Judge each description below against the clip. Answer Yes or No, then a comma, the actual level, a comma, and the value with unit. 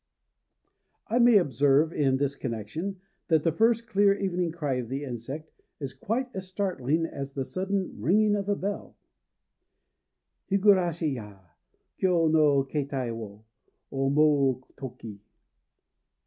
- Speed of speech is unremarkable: No, slow, 125 wpm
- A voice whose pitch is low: No, medium, 155 Hz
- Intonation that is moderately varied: No, wide, 6.2 semitones